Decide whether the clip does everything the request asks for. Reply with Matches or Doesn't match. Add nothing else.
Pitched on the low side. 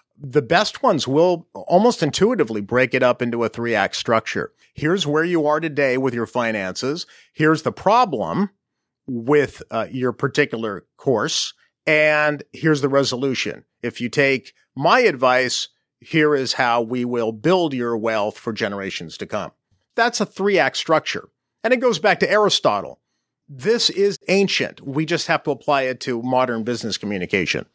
Doesn't match